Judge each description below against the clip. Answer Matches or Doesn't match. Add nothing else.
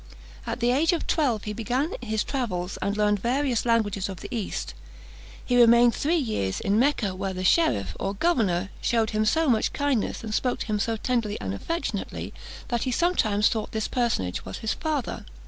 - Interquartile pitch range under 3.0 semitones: Doesn't match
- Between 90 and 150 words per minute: Doesn't match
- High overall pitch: Matches